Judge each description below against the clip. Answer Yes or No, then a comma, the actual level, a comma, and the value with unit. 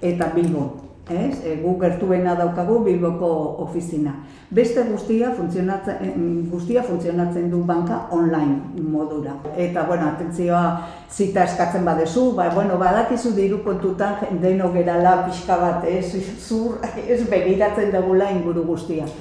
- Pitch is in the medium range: Yes, medium, 175 Hz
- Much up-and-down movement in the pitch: No, narrow, 2.6 semitones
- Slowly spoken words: Yes, slow, 120 wpm